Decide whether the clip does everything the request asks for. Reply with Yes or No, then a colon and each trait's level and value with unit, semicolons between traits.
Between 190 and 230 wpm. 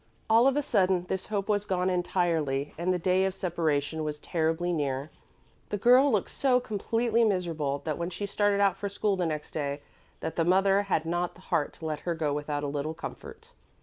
Yes: average, 200 wpm